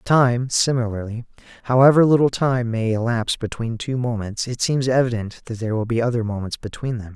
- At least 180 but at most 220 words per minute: Yes, average, 185 wpm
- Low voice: Yes, low, 120 Hz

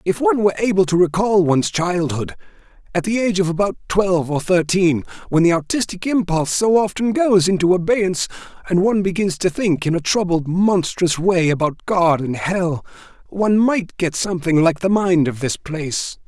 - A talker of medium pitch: Yes, medium, 180 Hz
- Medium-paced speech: Yes, average, 175 wpm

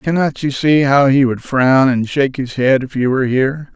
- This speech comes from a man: Yes, male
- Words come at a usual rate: No, fast, 240 wpm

